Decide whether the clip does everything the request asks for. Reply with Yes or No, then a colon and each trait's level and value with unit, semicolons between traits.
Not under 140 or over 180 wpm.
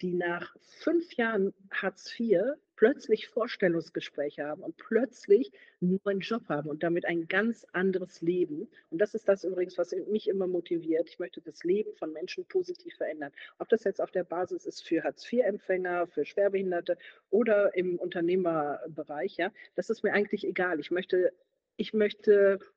Yes: average, 165 wpm